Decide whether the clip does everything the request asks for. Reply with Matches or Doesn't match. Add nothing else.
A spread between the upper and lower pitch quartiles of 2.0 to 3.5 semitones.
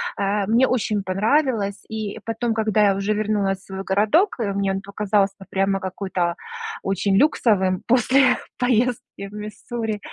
Matches